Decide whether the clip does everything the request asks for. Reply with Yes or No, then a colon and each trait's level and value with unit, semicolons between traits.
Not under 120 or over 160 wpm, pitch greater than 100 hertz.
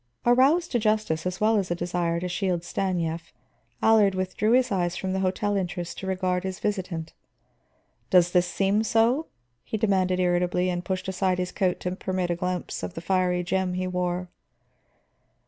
No: average, 175 wpm; medium, 185 Hz